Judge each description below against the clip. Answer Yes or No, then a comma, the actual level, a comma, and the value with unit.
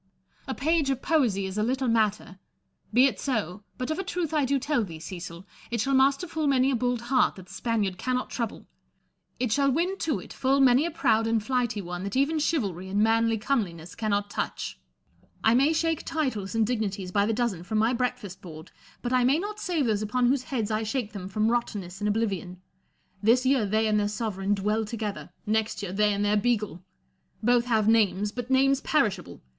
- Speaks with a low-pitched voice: No, high, 225 Hz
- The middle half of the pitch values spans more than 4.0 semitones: Yes, average, 4.4 semitones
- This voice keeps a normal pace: No, fast, 210 wpm